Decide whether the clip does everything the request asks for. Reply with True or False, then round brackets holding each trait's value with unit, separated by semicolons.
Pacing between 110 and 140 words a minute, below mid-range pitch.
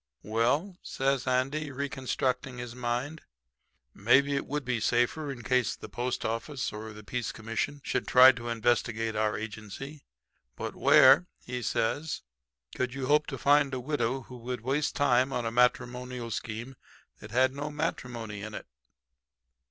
False (155 wpm; 125 Hz)